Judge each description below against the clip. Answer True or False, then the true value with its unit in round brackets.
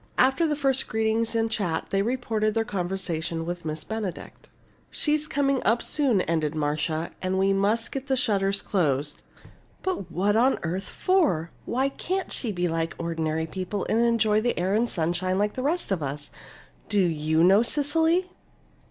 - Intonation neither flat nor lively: False (6.4 semitones)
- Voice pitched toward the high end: True (200 Hz)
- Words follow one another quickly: False (170 wpm)